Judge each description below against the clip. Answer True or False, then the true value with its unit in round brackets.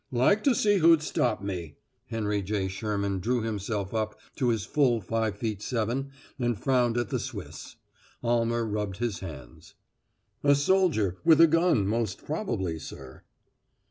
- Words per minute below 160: True (150 wpm)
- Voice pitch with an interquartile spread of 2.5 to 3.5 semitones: False (4.6 semitones)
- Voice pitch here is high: False (115 Hz)